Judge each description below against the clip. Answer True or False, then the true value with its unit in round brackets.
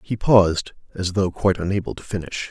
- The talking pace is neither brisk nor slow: True (190 wpm)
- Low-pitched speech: True (95 Hz)